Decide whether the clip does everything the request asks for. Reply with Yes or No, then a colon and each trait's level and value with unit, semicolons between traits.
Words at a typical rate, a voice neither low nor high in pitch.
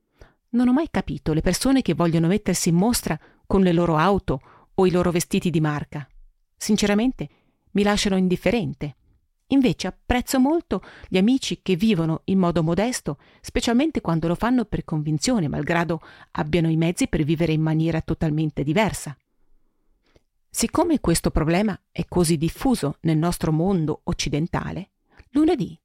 Yes: average, 145 wpm; medium, 175 Hz